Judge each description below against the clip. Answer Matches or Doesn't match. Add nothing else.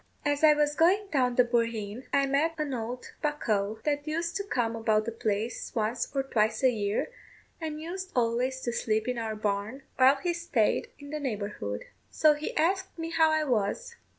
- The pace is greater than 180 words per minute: Matches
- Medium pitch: Doesn't match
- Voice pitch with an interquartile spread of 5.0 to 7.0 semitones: Matches